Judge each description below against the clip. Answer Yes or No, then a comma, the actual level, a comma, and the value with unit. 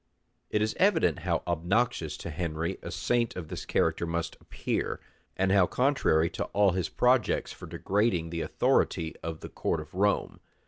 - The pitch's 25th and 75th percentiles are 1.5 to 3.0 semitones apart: No, average, 4.5 semitones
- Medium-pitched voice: No, very low, 90 Hz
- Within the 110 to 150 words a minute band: No, average, 170 wpm